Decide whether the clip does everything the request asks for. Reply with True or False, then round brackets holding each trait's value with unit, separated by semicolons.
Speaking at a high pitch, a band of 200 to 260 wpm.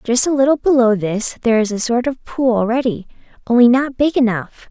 True (240 Hz; 205 wpm)